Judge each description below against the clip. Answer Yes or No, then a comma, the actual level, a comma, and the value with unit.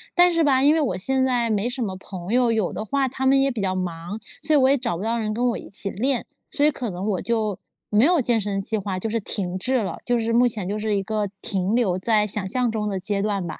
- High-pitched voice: Yes, high, 220 Hz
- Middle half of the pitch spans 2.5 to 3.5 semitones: No, average, 4.3 semitones